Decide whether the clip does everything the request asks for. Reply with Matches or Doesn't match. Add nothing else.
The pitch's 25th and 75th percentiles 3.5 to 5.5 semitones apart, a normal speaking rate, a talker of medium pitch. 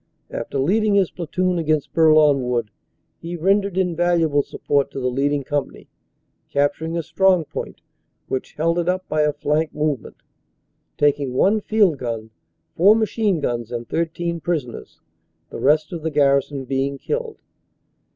Matches